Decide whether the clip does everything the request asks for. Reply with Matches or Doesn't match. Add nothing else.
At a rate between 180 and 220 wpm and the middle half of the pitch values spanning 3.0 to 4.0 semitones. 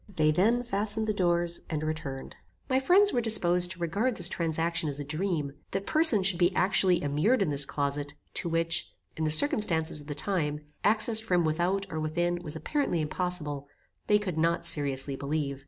Doesn't match